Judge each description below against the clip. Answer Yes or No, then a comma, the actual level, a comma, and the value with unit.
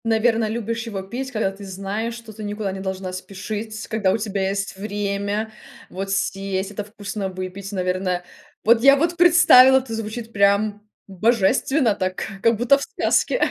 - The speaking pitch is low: No, high, 210 Hz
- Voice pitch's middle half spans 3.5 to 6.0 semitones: No, average, 2.8 semitones